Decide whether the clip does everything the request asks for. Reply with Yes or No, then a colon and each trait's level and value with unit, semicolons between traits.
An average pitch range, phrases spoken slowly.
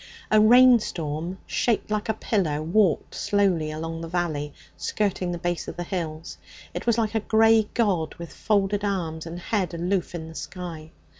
No: average, 4.5 semitones; average, 170 wpm